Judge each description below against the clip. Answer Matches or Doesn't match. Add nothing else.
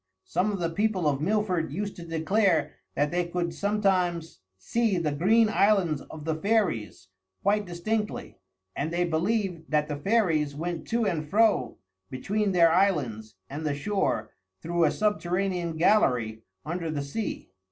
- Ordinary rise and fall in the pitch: Matches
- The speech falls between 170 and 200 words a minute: Doesn't match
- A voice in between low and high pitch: Matches